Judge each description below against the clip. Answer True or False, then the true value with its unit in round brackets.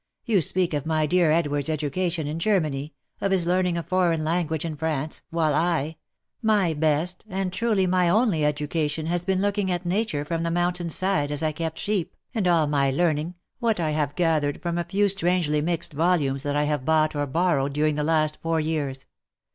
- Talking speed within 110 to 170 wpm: False (205 wpm)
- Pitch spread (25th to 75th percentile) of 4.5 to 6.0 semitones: False (3.2 semitones)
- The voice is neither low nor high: True (165 Hz)